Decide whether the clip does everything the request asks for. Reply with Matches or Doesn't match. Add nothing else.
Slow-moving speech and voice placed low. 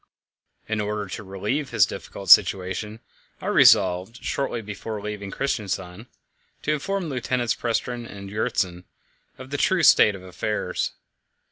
Matches